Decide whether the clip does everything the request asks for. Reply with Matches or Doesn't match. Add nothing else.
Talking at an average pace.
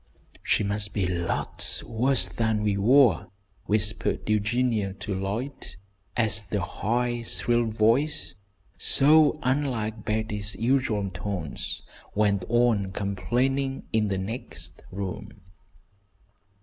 Doesn't match